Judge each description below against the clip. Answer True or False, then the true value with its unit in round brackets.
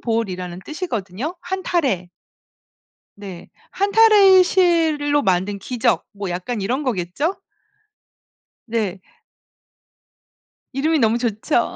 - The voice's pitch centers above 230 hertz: True (240 Hz)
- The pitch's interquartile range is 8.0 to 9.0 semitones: True (8.6 semitones)